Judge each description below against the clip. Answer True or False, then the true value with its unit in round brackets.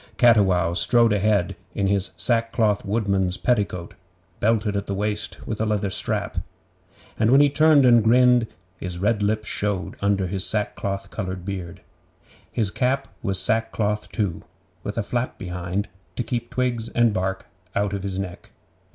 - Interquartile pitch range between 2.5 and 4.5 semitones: True (2.9 semitones)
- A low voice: True (105 Hz)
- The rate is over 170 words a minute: False (155 wpm)